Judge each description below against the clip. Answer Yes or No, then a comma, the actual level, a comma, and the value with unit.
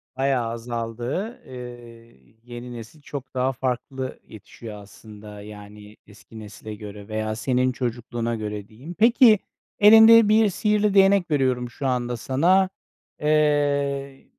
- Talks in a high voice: No, low, 125 Hz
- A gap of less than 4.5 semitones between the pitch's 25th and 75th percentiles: No, average, 5.0 semitones